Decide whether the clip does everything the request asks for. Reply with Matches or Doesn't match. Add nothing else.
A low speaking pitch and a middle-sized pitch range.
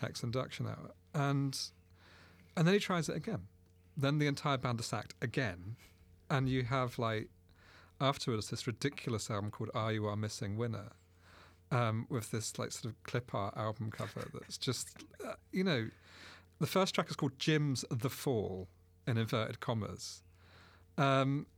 Doesn't match